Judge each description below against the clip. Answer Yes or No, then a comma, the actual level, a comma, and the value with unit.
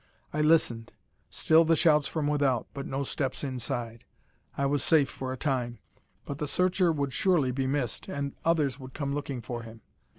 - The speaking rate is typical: Yes, average, 185 wpm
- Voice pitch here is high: No, medium, 140 Hz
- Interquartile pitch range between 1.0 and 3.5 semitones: Yes, average, 2.8 semitones